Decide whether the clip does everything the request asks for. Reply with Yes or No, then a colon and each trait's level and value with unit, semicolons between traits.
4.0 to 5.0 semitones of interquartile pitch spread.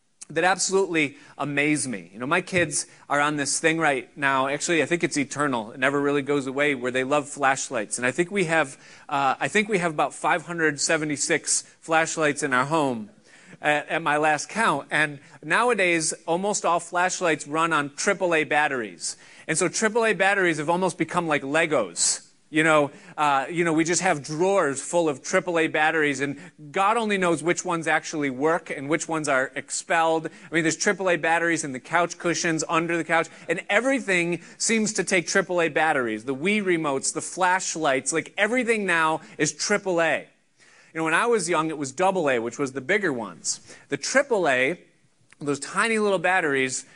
No: average, 3.3 semitones